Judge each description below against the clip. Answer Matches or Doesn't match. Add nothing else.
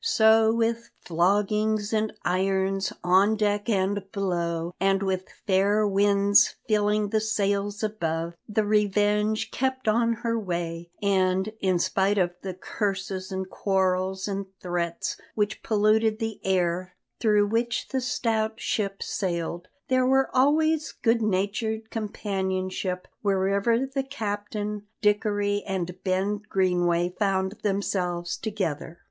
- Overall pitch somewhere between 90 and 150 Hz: Doesn't match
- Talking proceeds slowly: Matches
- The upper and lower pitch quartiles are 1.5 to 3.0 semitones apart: Matches